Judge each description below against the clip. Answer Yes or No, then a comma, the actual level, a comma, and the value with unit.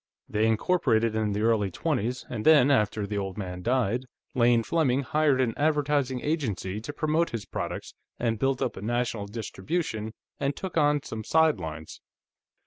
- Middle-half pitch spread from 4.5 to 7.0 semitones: Yes, wide, 5.4 semitones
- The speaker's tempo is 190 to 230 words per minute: No, average, 160 wpm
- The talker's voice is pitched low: Yes, low, 120 Hz